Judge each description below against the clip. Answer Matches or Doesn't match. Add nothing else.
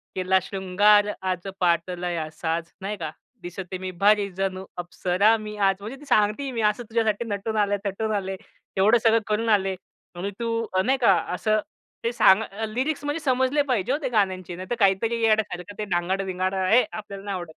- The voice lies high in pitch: Matches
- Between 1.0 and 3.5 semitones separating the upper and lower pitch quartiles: Matches